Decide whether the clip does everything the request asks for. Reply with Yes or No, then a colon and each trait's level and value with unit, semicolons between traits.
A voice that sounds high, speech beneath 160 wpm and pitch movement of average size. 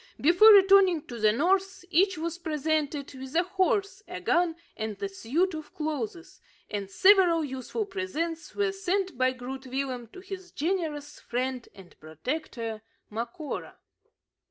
No: very high, 315 Hz; average, 140 wpm; wide, 6.4 semitones